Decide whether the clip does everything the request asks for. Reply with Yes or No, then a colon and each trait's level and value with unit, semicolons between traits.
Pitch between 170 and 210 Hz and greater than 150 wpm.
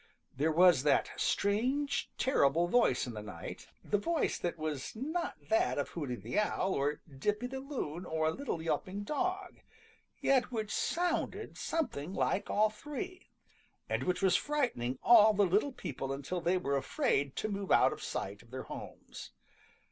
Yes: high, 190 Hz; average, 165 wpm